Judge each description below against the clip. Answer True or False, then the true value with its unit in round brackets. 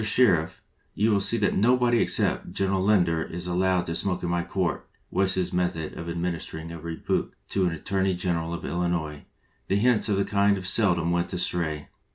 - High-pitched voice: False (90 Hz)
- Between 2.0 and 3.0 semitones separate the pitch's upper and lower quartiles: True (2.7 semitones)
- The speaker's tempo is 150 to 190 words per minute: False (200 wpm)